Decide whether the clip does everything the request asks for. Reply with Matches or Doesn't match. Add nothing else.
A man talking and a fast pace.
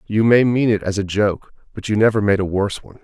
Matches